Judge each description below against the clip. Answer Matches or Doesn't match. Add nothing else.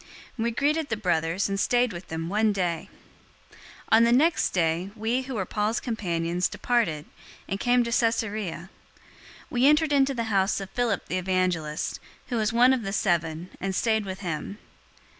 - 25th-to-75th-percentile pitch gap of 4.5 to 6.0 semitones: Matches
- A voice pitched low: Doesn't match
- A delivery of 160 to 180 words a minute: Matches